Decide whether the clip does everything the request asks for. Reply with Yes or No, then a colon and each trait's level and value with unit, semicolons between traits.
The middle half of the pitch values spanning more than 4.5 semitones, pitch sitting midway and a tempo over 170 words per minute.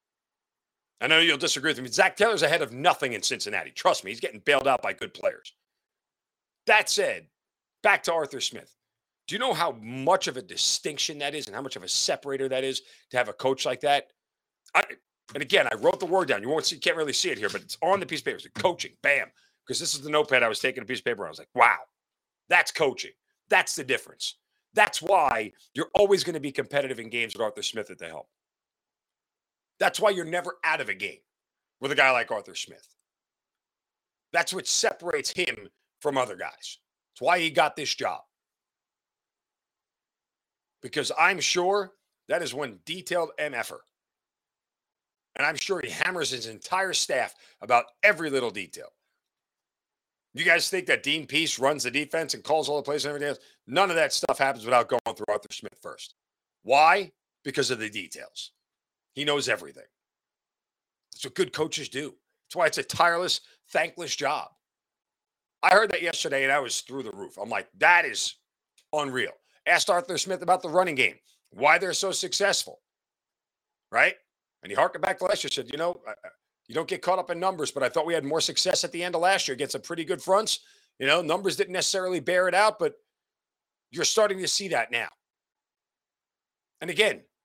Yes: average, 5.0 semitones; medium, 170 Hz; average, 200 wpm